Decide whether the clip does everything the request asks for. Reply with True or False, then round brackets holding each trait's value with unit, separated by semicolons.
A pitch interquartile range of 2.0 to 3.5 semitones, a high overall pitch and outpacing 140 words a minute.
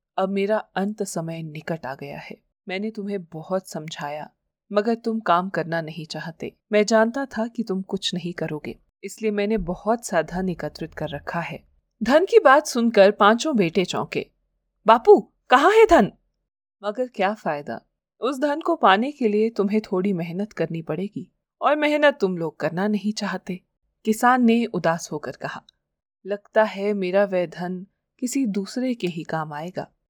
False (4.8 semitones; 195 Hz; 165 wpm)